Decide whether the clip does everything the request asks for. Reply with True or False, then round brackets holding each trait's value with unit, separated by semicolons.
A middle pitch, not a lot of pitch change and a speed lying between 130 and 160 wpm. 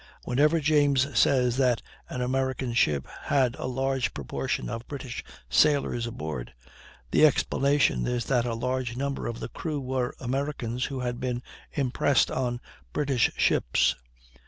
False (130 Hz; 2.3 semitones; 140 wpm)